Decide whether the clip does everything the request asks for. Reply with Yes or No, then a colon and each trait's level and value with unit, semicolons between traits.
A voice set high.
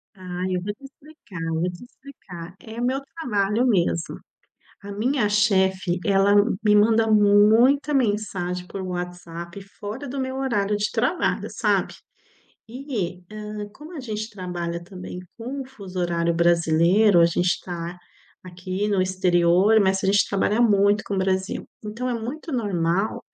Yes: high, 200 Hz